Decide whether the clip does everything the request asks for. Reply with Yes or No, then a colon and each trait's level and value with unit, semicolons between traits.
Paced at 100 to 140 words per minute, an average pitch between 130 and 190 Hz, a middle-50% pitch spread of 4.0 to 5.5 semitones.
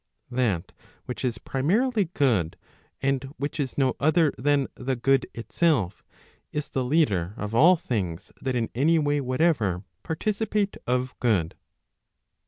Yes: slow, 135 wpm; low, 135 Hz; average, 5.2 semitones